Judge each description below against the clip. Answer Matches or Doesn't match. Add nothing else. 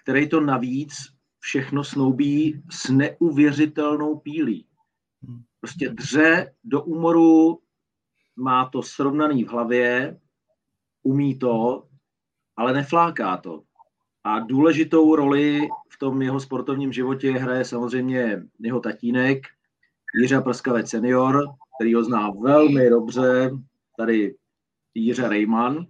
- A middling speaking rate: Doesn't match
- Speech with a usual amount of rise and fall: Matches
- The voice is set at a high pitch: Doesn't match